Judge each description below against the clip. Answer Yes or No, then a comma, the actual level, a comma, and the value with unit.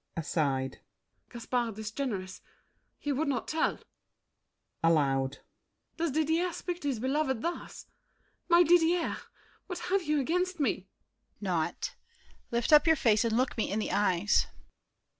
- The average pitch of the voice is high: Yes, very high, 260 Hz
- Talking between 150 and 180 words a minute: No, average, 140 wpm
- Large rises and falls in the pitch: Yes, wide, 7.9 semitones